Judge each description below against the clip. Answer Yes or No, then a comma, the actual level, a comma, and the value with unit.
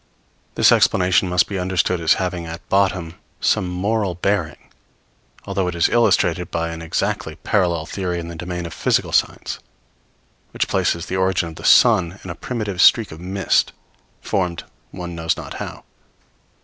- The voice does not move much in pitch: Yes, narrow, 2.0 semitones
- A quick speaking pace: No, average, 160 wpm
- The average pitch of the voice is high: No, very low, 90 Hz